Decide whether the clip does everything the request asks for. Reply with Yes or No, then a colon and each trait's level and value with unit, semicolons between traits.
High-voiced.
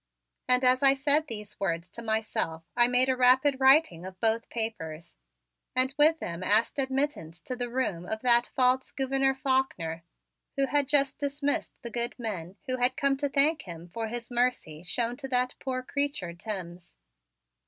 Yes: very high, 250 Hz